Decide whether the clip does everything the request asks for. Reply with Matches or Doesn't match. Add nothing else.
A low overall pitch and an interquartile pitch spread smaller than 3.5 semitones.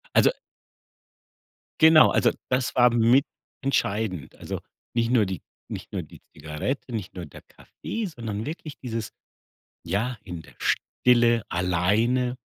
Doesn't match